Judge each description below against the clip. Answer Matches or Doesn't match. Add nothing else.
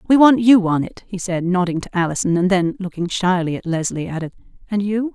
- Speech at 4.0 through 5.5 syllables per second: Doesn't match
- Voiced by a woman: Matches